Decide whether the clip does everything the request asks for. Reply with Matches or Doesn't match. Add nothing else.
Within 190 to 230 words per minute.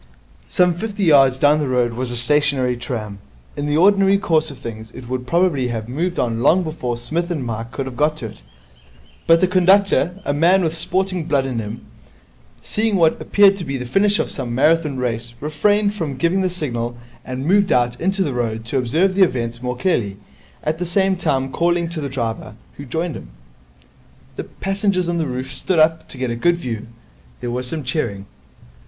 Matches